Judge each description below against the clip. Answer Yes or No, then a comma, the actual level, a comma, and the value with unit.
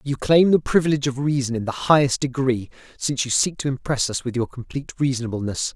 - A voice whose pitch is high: No, low, 135 Hz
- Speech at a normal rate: No, fast, 210 wpm